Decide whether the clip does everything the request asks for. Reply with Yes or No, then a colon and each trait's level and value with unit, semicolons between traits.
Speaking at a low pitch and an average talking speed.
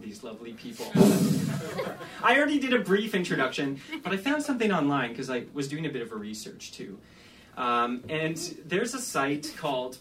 No: medium, 155 Hz; average, 180 wpm